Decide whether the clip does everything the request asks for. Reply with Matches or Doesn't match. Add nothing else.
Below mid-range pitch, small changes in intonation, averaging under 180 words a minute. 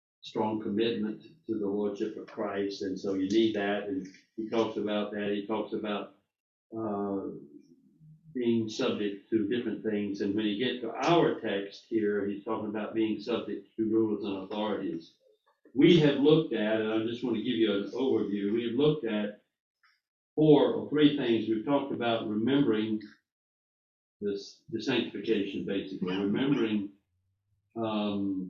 Matches